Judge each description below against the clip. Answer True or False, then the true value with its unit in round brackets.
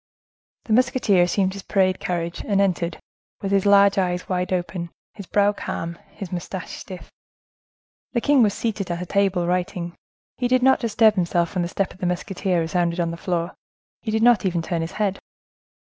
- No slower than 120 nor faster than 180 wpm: False (190 wpm)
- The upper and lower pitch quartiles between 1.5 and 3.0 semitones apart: True (2.6 semitones)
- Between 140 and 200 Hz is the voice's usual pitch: True (185 Hz)